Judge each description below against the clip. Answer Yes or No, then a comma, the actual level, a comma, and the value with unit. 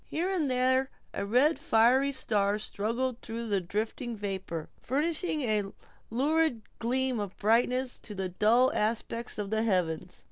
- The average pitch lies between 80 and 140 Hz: No, high, 230 Hz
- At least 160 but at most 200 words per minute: No, average, 150 wpm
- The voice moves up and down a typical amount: Yes, average, 4.0 semitones